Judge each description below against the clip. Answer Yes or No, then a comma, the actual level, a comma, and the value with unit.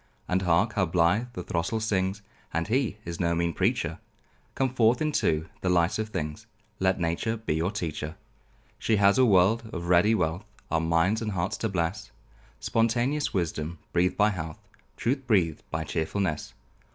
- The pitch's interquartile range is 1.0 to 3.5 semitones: No, average, 4.7 semitones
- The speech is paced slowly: No, average, 165 wpm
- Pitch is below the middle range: Yes, very low, 95 Hz